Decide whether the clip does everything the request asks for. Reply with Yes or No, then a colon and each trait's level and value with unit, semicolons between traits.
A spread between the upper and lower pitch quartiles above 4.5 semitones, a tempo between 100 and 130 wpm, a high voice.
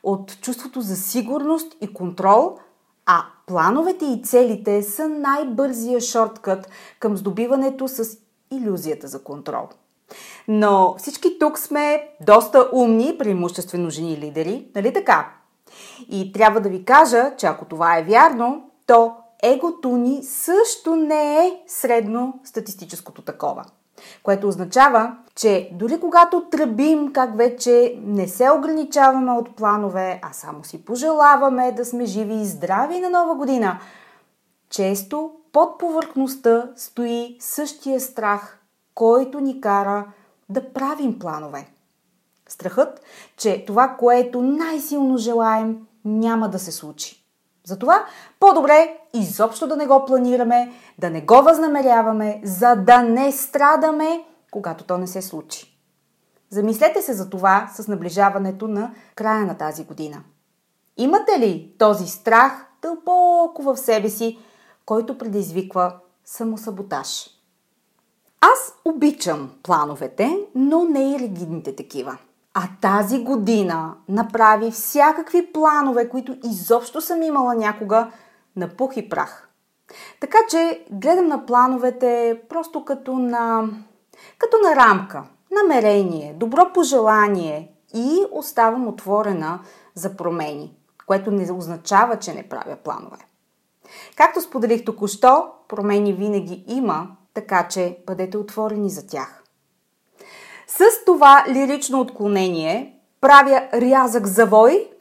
Yes: wide, 5.6 semitones; average, 120 wpm; high, 230 Hz